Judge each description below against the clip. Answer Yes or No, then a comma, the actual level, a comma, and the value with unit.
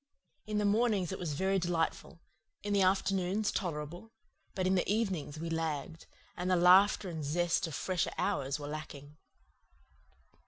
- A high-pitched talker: No, medium, 180 Hz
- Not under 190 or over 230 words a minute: No, average, 155 wpm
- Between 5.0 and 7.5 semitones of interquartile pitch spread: No, average, 3.6 semitones